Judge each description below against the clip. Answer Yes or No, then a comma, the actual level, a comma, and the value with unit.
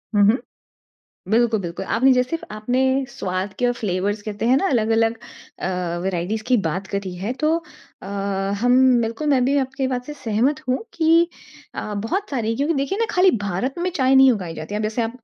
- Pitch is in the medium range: No, high, 240 Hz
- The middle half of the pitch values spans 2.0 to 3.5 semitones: No, average, 4.2 semitones